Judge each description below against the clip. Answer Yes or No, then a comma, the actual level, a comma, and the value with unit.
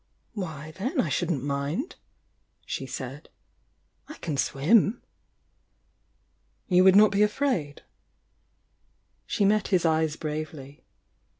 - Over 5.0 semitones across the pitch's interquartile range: Yes, wide, 5.6 semitones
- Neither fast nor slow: No, slow, 110 wpm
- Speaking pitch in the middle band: Yes, medium, 170 Hz